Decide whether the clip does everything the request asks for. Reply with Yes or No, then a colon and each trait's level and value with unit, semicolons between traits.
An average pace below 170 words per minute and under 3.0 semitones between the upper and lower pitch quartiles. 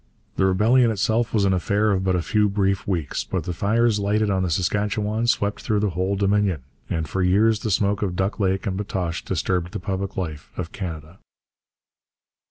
No: average, 190 wpm; narrow, 2.4 semitones